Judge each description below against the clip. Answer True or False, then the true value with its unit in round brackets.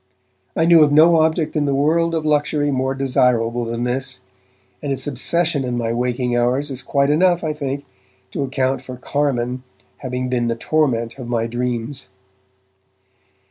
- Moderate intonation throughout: True (3.3 semitones)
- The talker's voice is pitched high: False (135 Hz)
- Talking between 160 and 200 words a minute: True (165 wpm)